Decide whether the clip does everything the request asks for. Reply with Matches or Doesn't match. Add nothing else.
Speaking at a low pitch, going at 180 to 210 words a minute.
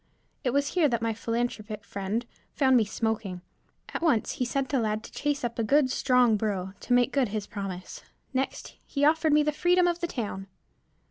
Doesn't match